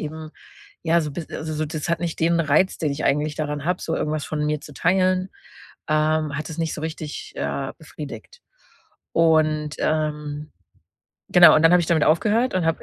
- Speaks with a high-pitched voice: No, medium, 155 Hz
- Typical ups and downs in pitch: No, narrow, 1.7 semitones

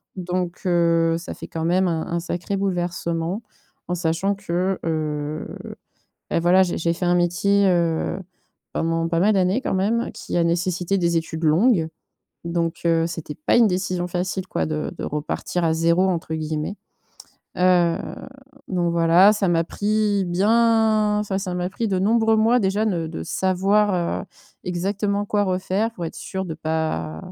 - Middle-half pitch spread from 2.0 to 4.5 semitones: Yes, average, 2.9 semitones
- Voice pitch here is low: No, medium, 180 Hz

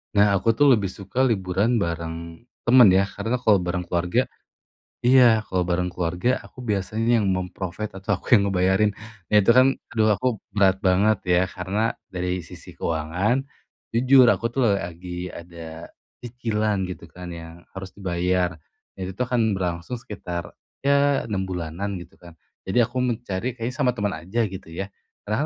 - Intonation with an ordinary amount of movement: Yes, average, 3.7 semitones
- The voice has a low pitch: Yes, very low, 95 Hz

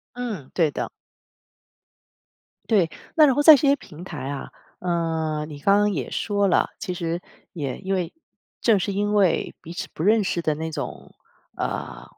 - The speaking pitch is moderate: Yes, medium, 180 Hz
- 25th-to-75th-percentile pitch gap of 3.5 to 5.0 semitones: Yes, average, 4.4 semitones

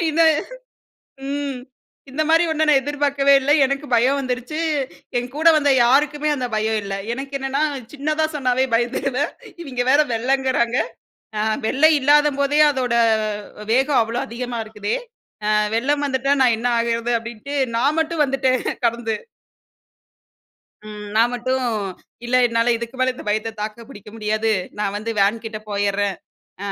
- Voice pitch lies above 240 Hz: Yes, very high, 255 Hz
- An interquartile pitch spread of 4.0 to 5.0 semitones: No, average, 3.5 semitones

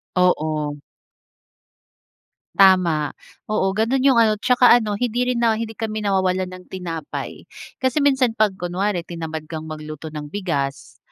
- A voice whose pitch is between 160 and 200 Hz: Yes, high, 190 Hz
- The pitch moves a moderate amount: No, wide, 6.0 semitones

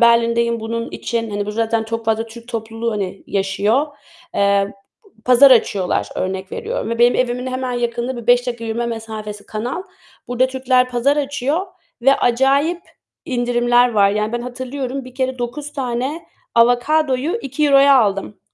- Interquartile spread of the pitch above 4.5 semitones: No, narrow, 2.5 semitones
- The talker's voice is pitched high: Yes, high, 240 Hz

